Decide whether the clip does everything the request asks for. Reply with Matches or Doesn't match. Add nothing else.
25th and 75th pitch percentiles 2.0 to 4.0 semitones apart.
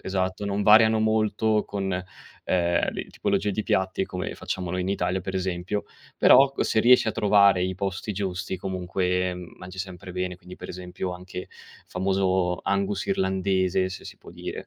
Doesn't match